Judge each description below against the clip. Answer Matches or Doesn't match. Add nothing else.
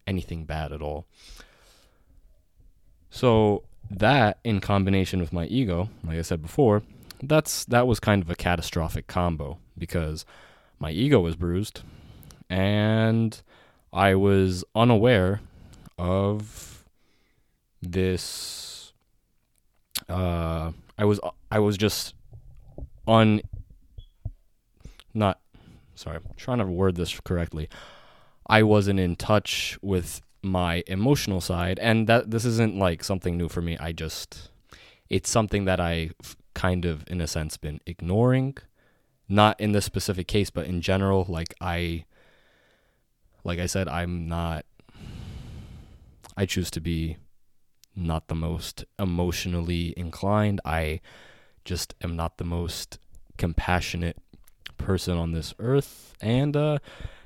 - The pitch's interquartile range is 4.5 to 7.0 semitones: Doesn't match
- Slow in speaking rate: Matches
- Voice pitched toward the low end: Matches